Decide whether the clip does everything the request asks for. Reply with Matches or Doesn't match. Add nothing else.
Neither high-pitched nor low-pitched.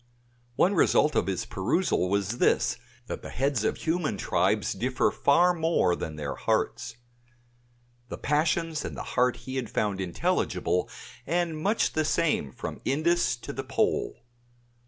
Doesn't match